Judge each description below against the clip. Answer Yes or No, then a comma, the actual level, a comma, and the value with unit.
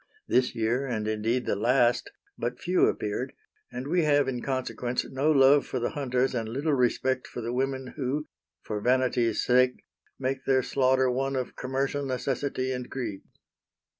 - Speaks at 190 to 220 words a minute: No, average, 165 wpm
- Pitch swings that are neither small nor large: No, narrow, 1.8 semitones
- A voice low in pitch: Yes, low, 130 Hz